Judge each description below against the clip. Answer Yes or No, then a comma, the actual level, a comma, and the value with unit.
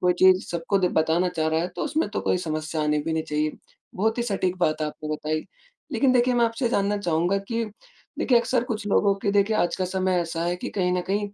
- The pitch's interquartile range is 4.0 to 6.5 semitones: Yes, average, 4.3 semitones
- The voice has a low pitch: No, medium, 185 Hz